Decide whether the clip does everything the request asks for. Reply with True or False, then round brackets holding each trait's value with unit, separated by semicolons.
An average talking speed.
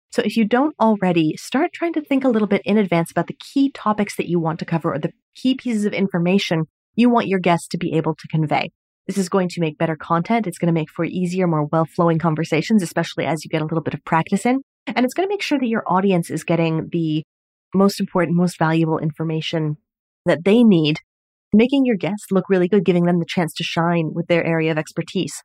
False (240 wpm)